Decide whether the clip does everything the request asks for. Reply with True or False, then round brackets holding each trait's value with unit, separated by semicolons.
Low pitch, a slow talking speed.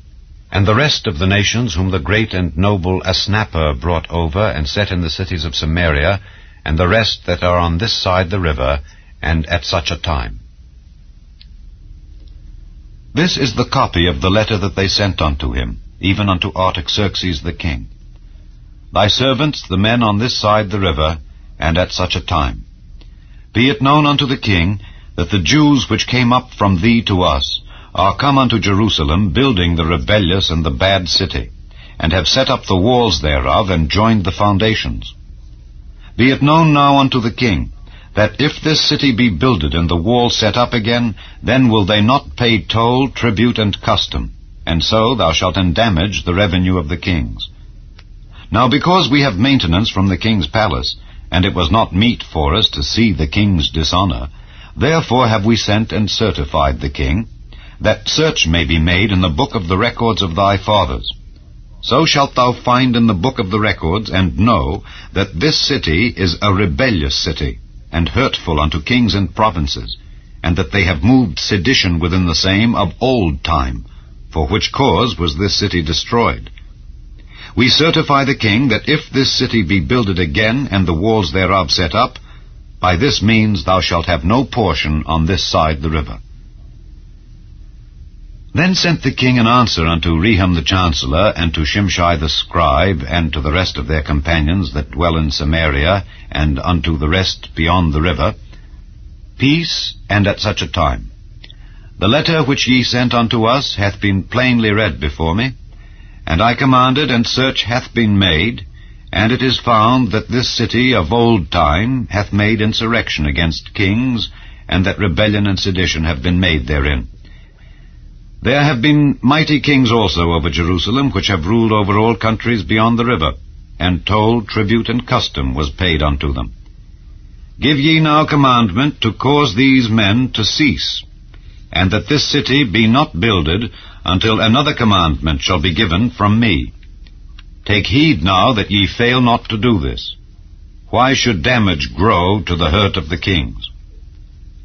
False (95 Hz; 170 wpm)